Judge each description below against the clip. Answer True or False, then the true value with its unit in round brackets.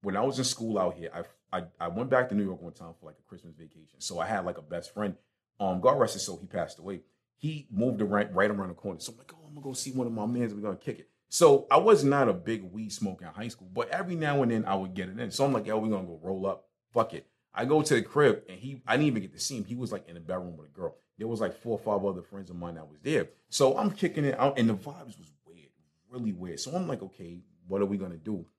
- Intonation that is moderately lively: False (5.9 semitones)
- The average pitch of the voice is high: False (105 Hz)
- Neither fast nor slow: False (320 wpm)